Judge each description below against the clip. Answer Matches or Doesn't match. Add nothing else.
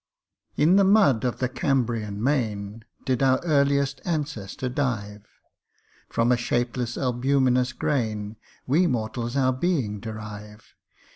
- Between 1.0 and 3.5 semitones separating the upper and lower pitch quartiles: Doesn't match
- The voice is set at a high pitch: Doesn't match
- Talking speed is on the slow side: Matches